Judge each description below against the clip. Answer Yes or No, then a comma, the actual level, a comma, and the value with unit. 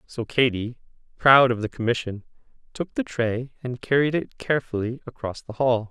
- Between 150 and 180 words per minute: Yes, average, 160 wpm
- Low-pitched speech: Yes, low, 120 Hz